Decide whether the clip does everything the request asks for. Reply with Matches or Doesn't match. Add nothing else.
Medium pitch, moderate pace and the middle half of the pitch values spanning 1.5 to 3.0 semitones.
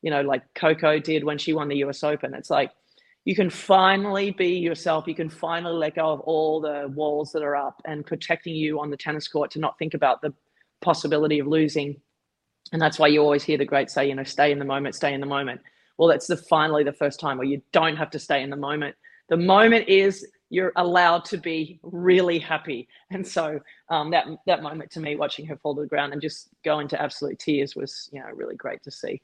Doesn't match